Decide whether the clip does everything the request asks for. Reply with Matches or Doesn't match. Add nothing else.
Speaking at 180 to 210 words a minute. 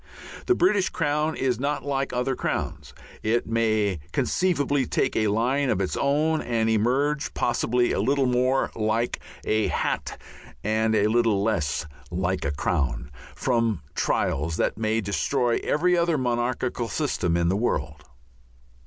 Doesn't match